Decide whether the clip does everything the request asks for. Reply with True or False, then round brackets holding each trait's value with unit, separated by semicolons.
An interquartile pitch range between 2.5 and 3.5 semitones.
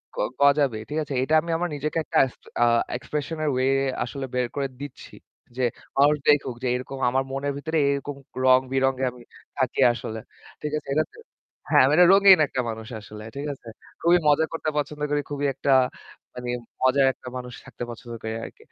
True (2.8 semitones)